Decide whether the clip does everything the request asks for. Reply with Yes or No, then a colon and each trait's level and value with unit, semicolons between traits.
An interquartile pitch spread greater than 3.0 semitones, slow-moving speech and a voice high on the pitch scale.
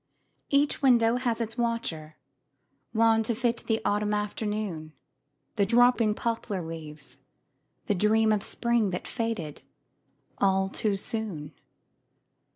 Yes: average, 3.4 semitones; slow, 115 wpm; high, 215 Hz